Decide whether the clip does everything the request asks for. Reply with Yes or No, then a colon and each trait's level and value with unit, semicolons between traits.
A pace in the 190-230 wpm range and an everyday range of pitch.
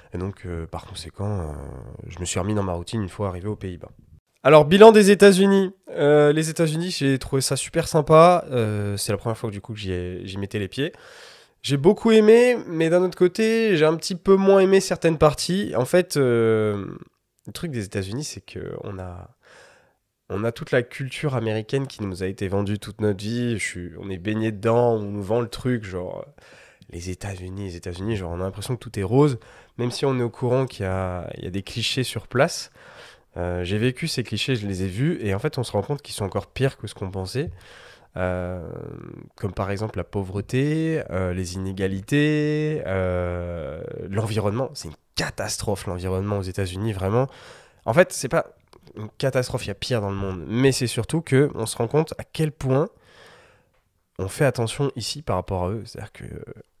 No: average, 210 wpm; wide, 6.8 semitones